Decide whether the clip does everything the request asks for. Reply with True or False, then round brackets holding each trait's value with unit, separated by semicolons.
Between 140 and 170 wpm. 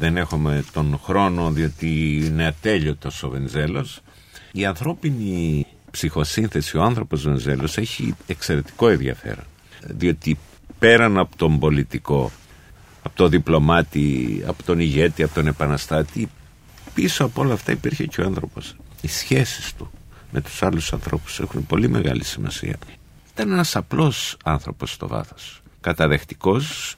False (130 wpm)